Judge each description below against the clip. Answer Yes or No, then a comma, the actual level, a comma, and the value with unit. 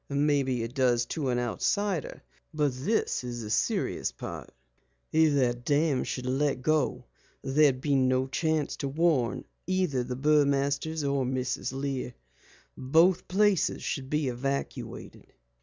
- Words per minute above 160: No, slow, 135 wpm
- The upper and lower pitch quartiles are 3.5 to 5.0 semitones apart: No, average, 3.1 semitones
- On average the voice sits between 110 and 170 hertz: Yes, medium, 140 Hz